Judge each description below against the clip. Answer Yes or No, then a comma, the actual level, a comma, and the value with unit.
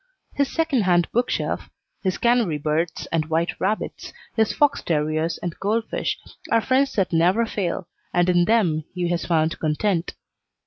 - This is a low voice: No, medium, 180 Hz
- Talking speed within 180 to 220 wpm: No, average, 150 wpm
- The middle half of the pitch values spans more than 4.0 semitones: Yes, average, 5.2 semitones